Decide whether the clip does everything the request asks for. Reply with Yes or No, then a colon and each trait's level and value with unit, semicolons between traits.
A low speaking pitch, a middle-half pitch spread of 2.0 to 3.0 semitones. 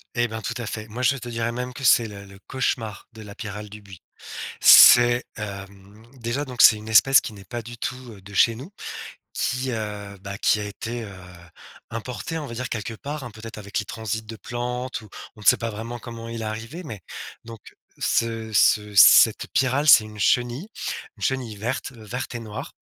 Yes: low, 115 Hz; narrow, 2.5 semitones